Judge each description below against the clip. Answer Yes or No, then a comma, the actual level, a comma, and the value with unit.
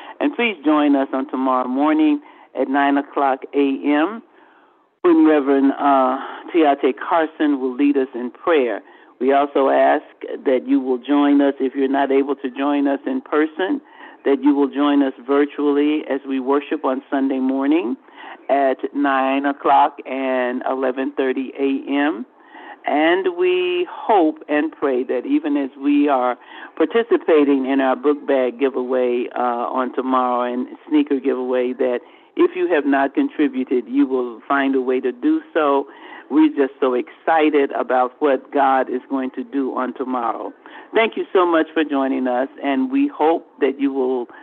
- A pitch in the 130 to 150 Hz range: Yes, medium, 140 Hz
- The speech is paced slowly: No, average, 160 wpm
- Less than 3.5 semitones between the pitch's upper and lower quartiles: Yes, average, 2.8 semitones